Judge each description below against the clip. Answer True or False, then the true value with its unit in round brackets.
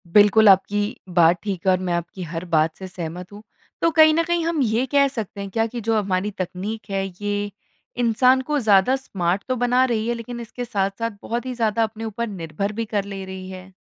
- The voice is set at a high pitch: True (210 Hz)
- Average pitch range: True (3.9 semitones)